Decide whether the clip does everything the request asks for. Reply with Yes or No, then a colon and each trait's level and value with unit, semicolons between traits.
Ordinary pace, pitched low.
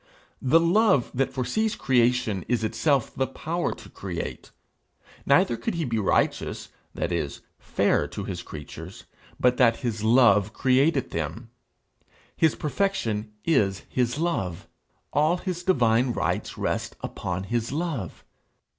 No: slow, 130 wpm; low, 125 Hz